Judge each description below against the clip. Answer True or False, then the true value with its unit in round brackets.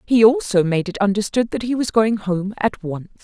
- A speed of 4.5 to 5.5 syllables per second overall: True (5.1 syllables/s)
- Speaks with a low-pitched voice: False (210 Hz)